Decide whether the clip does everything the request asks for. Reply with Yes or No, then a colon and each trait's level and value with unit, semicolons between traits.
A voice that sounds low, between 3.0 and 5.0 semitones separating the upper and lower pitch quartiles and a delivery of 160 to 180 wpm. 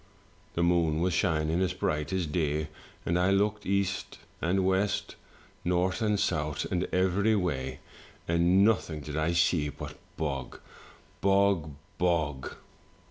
No: very low, 85 Hz; average, 3.6 semitones; slow, 135 wpm